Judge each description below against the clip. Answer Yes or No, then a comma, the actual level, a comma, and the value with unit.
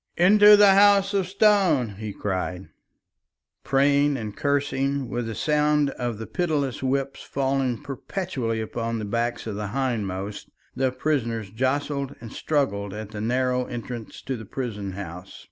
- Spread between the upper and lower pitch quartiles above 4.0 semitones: Yes, average, 4.5 semitones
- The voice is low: Yes, low, 130 Hz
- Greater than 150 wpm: No, average, 145 wpm